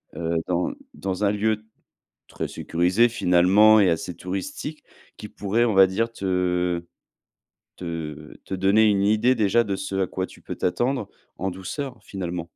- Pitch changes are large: No, average, 3.4 semitones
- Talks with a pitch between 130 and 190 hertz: No, very low, 95 Hz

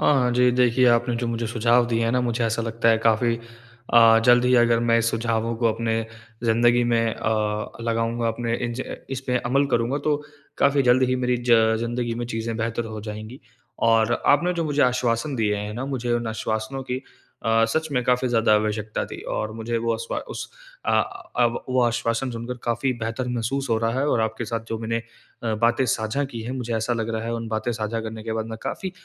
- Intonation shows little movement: Yes, narrow, 1.6 semitones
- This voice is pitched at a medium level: No, low, 115 Hz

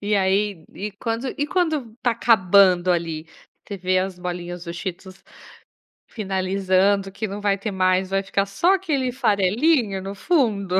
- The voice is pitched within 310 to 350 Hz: No, high, 195 Hz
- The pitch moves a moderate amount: Yes, average, 3.4 semitones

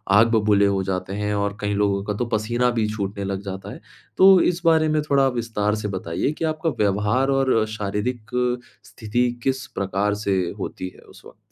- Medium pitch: No, low, 105 Hz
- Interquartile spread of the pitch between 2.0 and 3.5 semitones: No, average, 3.9 semitones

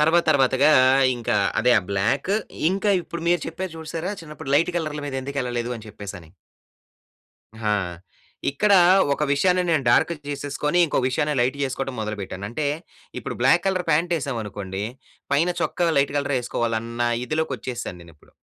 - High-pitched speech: No, medium, 140 Hz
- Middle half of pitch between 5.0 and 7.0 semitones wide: Yes, wide, 5.4 semitones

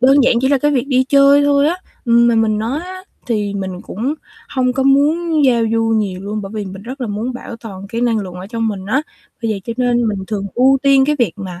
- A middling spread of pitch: Yes, average, 4.5 semitones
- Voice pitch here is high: Yes, high, 235 Hz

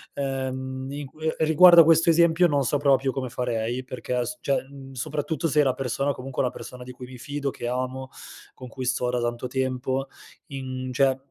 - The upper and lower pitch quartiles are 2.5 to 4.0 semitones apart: No, narrow, 2.1 semitones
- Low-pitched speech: Yes, low, 130 Hz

